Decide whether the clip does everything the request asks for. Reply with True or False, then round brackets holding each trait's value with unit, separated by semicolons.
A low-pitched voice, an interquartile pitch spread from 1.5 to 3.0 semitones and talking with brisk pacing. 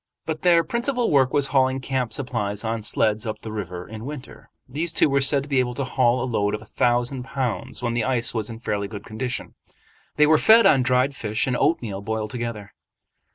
False (125 Hz; 3.8 semitones; 215 wpm)